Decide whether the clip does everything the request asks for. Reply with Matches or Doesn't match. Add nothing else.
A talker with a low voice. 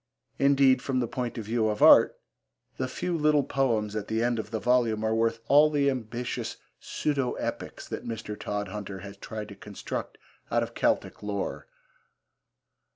Matches